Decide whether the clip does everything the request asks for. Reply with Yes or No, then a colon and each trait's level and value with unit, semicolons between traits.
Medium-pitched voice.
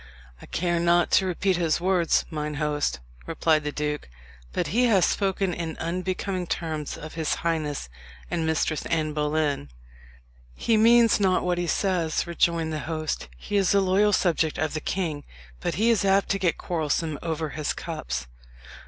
Yes: medium, 165 Hz